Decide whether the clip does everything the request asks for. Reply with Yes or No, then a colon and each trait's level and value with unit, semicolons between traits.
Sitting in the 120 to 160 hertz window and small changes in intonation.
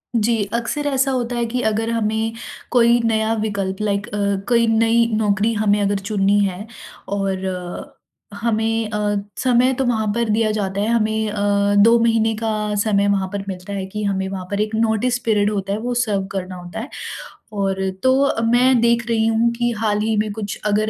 No: high, 220 Hz; narrow, 2.3 semitones